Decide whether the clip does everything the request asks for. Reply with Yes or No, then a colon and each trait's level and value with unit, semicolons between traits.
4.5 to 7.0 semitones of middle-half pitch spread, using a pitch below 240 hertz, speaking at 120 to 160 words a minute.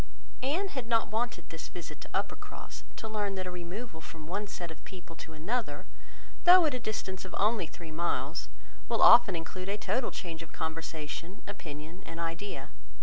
No: average, 5.1 semitones; medium, 185 Hz; average, 180 wpm